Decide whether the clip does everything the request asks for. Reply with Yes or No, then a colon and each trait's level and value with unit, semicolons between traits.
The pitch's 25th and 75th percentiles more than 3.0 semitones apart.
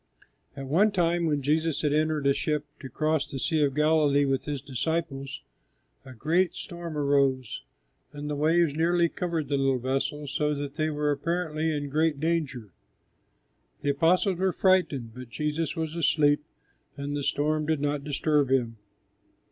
No: narrow, 2.6 semitones